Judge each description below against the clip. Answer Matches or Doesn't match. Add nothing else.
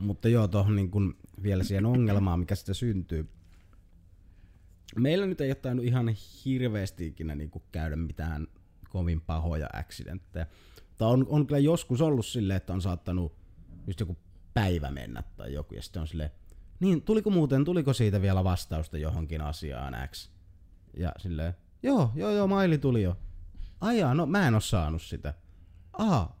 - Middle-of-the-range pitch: Doesn't match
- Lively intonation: Matches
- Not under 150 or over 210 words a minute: Matches